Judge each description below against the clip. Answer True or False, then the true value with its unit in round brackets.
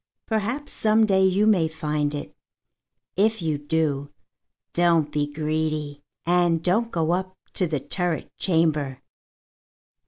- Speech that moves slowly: True (125 wpm)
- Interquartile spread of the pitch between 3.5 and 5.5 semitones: True (4.0 semitones)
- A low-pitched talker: False (165 Hz)